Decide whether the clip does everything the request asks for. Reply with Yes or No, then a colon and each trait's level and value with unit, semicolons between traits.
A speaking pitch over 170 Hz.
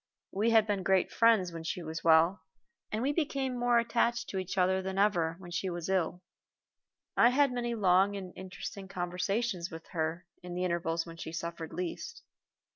Yes: medium, 185 Hz